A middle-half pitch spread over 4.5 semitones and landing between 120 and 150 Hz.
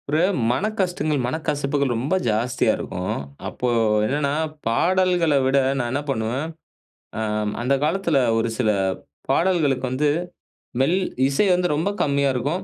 Yes: average, 4.9 semitones; medium, 140 Hz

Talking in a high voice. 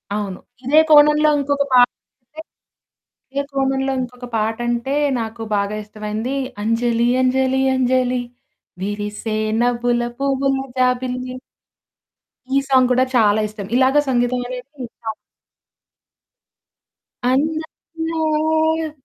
Yes: very high, 255 Hz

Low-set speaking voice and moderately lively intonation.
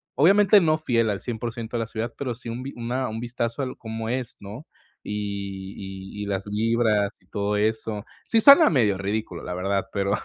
Yes: low, 110 Hz; average, 3.4 semitones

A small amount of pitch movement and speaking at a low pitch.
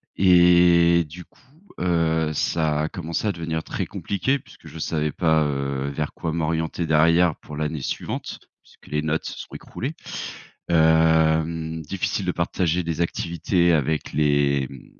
Yes: narrow, 2.0 semitones; very low, 80 Hz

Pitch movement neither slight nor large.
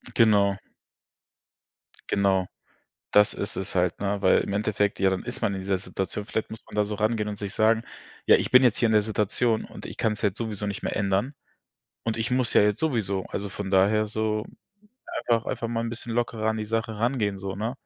No: narrow, 2.1 semitones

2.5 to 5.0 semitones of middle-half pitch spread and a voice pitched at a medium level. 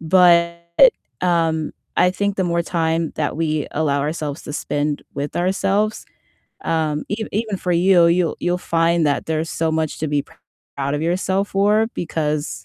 Yes: average, 2.9 semitones; medium, 165 Hz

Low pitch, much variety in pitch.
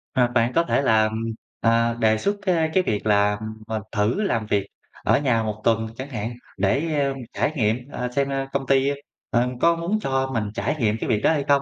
No: low, 120 Hz; average, 4.4 semitones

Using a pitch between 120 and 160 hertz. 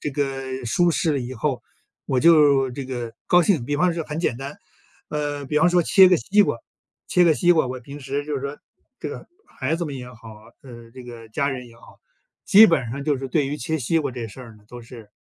Yes: medium, 140 Hz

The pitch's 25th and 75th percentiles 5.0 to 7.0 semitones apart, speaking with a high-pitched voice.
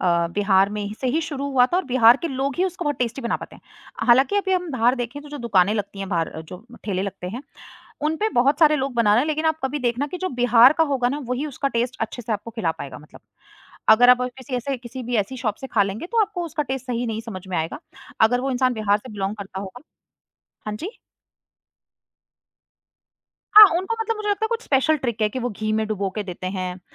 Yes: wide, 5.4 semitones; high, 245 Hz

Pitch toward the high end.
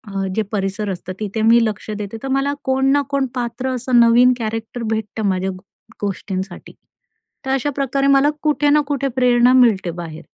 Yes: high, 235 Hz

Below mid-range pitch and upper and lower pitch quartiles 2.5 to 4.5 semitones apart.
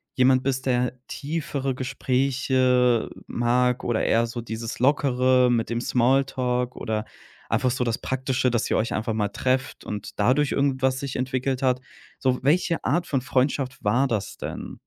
No: low, 125 Hz; narrow, 1.8 semitones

